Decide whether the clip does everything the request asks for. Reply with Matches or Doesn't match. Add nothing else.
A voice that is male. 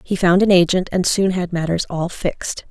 Doesn't match